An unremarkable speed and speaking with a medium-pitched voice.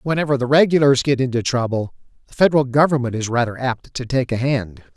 No: average, 195 wpm; low, 130 Hz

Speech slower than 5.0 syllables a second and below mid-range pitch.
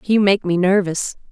No: 4.6 syllables/s; high, 190 Hz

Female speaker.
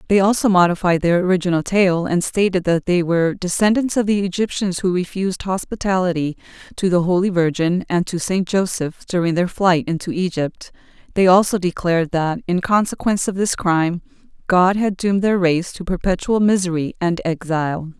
Yes: female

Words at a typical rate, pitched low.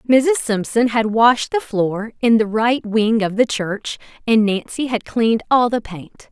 No: average, 190 wpm; high, 225 Hz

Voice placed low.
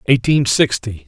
Yes: low, 120 Hz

